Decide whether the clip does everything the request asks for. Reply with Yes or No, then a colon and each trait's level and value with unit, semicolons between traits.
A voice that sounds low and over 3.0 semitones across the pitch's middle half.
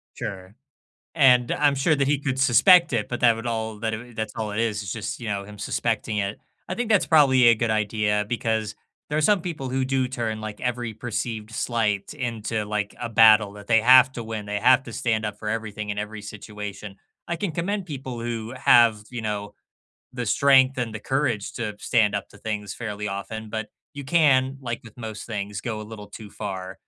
Yes: low, 115 Hz; average, 3.6 semitones